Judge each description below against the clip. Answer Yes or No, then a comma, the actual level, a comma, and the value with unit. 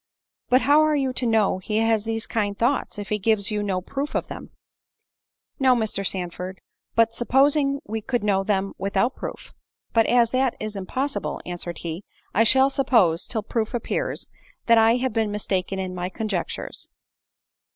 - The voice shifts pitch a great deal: No, average, 4.3 semitones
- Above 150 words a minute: Yes, average, 170 wpm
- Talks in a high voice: Yes, high, 220 Hz